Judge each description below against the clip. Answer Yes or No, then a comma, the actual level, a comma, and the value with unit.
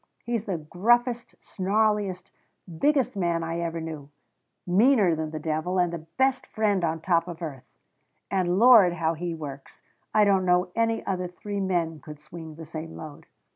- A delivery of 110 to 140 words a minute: No, average, 170 wpm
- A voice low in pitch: No, medium, 175 Hz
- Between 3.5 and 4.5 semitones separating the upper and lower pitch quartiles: Yes, average, 4.2 semitones